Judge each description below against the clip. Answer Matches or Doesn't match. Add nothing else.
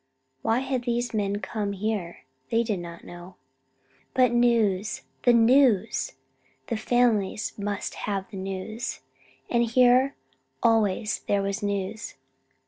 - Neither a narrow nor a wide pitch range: Matches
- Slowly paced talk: Matches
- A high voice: Matches